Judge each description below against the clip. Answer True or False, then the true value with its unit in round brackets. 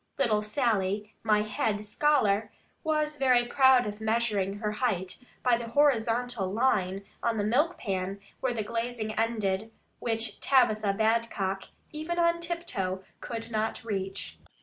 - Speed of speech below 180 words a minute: True (135 wpm)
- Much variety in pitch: False (3.3 semitones)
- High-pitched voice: True (225 Hz)